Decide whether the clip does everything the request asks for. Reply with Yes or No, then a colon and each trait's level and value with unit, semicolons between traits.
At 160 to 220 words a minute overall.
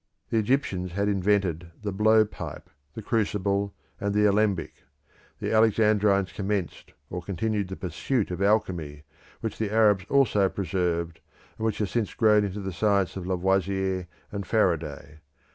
No: average, 145 wpm